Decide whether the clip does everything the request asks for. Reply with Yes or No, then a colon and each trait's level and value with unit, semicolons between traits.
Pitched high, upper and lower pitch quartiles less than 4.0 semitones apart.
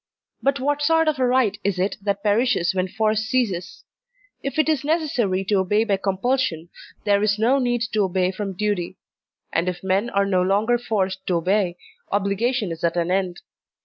No: high, 205 Hz; average, 4.5 semitones